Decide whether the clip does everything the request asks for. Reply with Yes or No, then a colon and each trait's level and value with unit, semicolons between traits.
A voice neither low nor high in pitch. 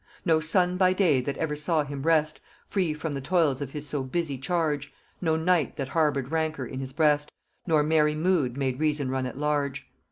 Yes: medium, 150 Hz